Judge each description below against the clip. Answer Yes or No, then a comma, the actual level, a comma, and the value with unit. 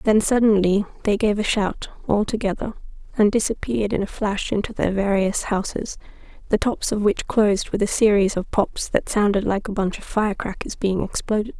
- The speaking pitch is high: Yes, high, 205 Hz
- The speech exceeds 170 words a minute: Yes, average, 185 wpm